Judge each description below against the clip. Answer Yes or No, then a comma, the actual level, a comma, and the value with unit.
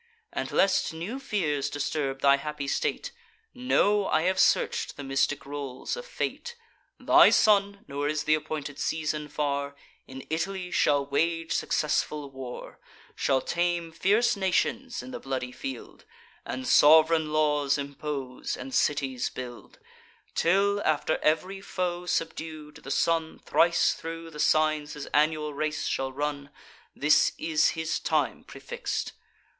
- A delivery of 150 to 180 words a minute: No, slow, 135 wpm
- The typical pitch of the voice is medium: Yes, medium, 155 Hz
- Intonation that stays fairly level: No, average, 3.8 semitones